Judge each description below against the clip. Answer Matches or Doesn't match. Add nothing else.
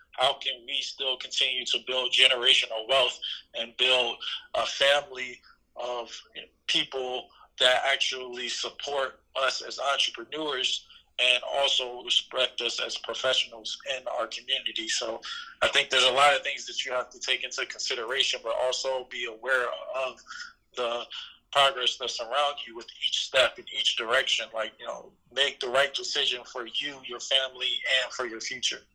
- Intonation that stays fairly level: Matches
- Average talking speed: Matches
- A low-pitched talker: Matches